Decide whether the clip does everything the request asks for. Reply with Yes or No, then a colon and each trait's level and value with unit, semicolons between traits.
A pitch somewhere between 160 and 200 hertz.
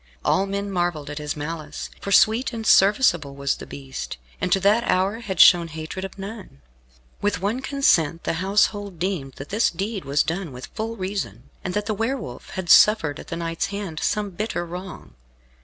Yes: high, 190 Hz